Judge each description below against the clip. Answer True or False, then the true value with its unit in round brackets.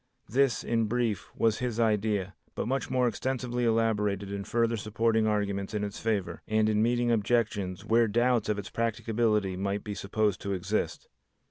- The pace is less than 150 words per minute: False (165 wpm)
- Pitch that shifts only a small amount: True (2.3 semitones)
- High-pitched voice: False (110 Hz)